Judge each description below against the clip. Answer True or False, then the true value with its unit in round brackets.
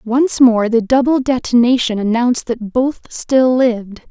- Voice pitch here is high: True (240 Hz)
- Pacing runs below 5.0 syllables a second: True (4.4 syllables/s)